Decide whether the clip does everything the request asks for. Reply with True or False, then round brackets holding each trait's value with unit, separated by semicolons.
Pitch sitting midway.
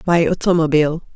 True (160 Hz)